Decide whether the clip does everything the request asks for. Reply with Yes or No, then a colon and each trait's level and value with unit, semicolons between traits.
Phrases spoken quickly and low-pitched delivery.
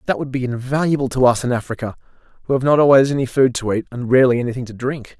Yes: fast, 245 wpm; low, 130 Hz